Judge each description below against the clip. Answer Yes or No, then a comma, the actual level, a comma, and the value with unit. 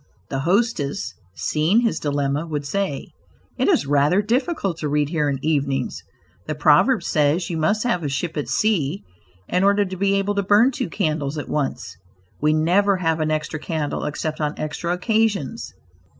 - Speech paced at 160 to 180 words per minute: Yes, average, 170 wpm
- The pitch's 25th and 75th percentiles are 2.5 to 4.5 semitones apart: No, average, 5.1 semitones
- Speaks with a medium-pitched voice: Yes, medium, 160 Hz